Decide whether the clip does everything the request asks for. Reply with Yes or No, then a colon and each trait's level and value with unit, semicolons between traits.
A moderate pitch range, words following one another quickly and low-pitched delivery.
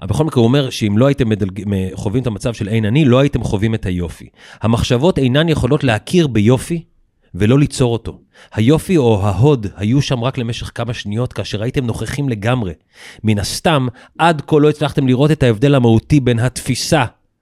Yes: average, 4.7 semitones; fast, 180 wpm; low, 125 Hz